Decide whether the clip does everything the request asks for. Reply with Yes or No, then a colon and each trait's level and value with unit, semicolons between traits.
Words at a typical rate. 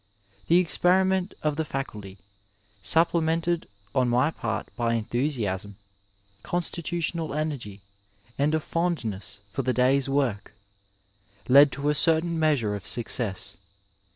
No: slow, 120 wpm